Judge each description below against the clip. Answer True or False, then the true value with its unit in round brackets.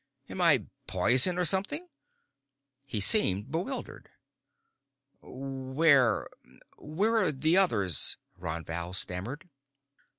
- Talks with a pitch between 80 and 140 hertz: True (135 Hz)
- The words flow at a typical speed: False (95 wpm)